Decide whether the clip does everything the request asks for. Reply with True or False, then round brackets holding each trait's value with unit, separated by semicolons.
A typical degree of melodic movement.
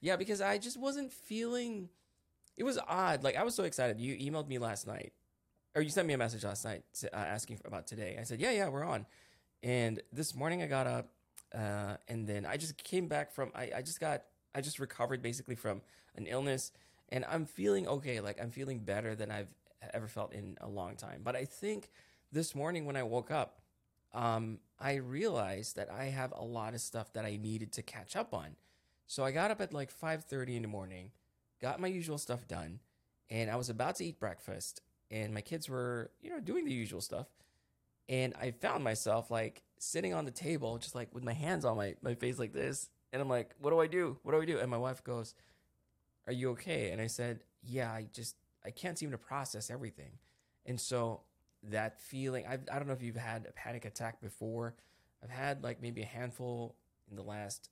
True (4.2 semitones)